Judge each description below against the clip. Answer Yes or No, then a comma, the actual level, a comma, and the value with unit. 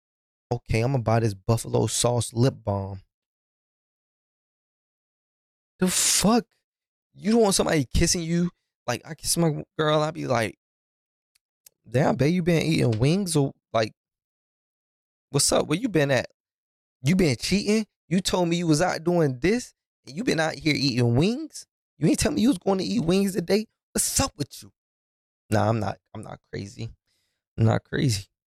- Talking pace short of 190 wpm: Yes, average, 170 wpm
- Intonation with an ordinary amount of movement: No, wide, 8.5 semitones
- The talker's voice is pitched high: No, medium, 140 Hz